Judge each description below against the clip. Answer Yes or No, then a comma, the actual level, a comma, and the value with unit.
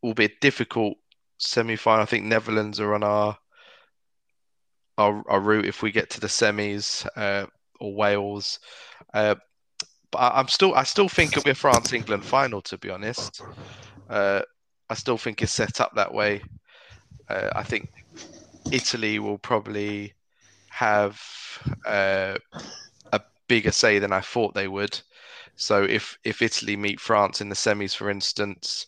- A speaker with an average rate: Yes, average, 160 wpm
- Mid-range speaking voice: No, low, 105 Hz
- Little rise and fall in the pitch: Yes, narrow, 1.7 semitones